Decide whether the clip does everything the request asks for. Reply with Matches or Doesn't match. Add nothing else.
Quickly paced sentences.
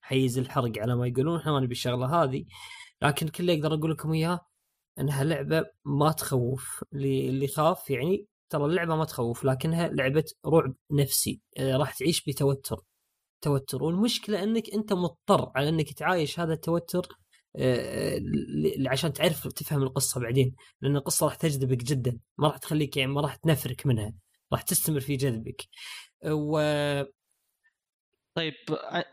Matches